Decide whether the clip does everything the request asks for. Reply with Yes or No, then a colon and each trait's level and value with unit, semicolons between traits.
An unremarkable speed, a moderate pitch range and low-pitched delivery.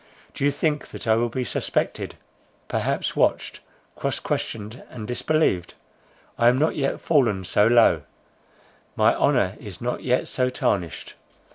Yes: average, 145 wpm; average, 4.0 semitones; low, 120 Hz